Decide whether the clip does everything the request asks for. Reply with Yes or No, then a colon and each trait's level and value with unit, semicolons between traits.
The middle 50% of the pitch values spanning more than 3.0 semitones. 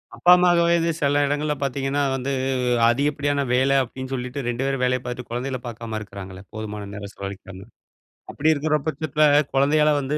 Yes: average, 3.7 semitones